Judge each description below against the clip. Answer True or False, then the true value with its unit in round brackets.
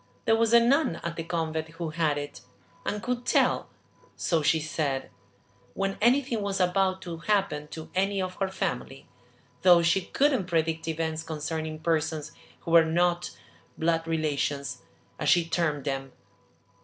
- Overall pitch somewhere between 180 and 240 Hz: False (165 Hz)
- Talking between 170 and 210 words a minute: False (155 wpm)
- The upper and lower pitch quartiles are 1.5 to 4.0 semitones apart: True (3.3 semitones)